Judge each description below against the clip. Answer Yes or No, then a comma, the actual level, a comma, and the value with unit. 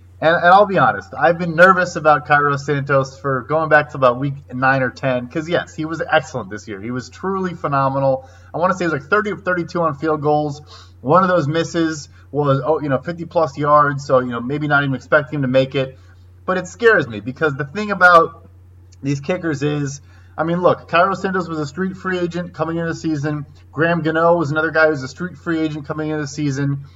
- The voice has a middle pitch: Yes, medium, 150 Hz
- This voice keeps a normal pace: No, fast, 235 wpm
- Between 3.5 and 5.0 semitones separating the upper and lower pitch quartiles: Yes, average, 3.9 semitones